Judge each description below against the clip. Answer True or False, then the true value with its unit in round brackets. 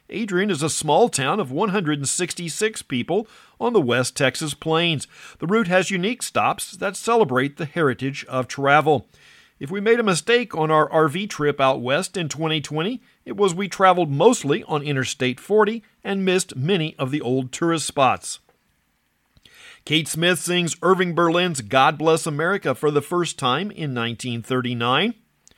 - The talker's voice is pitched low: False (160 Hz)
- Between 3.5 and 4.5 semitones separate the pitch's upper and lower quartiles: False (5.4 semitones)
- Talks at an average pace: True (155 wpm)